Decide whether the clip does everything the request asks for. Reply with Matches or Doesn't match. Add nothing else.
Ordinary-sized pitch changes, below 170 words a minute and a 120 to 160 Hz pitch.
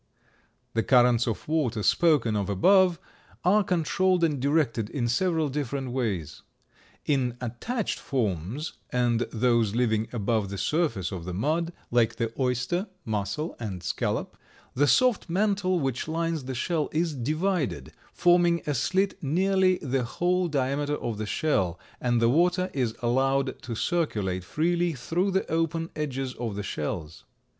Doesn't match